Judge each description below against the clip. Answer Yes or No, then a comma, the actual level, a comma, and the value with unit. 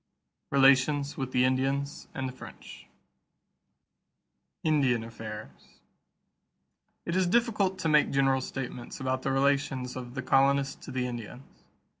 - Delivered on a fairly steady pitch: Yes, narrow, 1.7 semitones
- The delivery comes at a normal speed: No, slow, 125 wpm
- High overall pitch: No, low, 135 Hz